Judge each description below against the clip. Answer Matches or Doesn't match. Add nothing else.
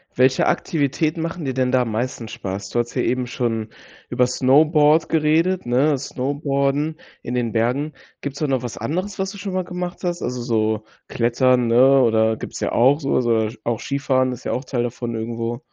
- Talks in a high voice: Doesn't match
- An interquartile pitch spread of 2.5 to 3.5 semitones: Doesn't match